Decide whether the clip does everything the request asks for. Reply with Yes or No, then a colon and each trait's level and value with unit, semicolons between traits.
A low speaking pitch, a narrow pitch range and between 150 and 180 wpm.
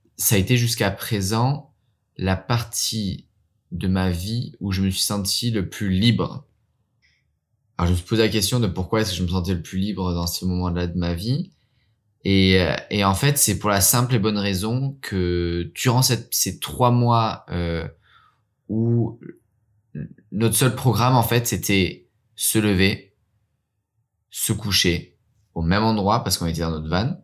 No: low, 105 Hz; average, 3.8 semitones; average, 175 wpm